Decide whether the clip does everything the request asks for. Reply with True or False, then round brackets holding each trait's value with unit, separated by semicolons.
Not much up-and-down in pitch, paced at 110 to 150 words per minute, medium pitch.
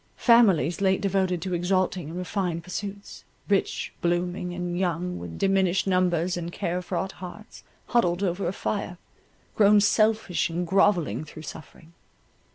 True (2.1 semitones; 140 wpm; 180 Hz)